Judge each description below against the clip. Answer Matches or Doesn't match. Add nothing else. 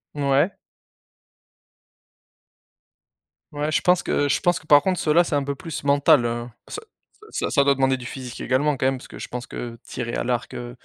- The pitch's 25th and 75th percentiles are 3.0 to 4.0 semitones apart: Matches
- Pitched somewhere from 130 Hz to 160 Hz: Matches